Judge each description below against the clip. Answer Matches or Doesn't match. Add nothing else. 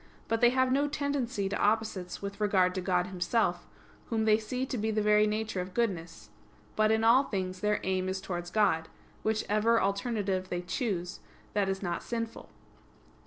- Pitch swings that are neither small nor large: Matches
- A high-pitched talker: Matches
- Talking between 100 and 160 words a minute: Doesn't match